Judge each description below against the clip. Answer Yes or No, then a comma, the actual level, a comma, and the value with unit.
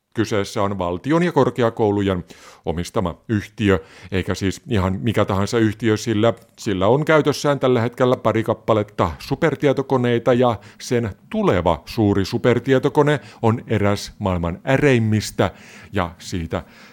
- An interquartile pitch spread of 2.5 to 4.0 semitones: No, average, 4.6 semitones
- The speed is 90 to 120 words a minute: Yes, average, 115 wpm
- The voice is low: Yes, low, 110 Hz